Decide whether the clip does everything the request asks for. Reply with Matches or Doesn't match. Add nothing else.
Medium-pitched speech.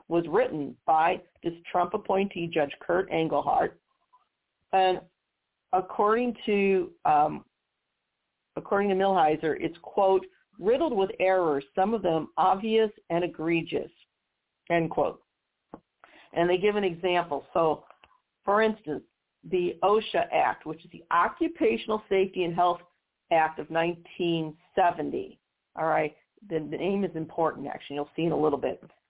Matches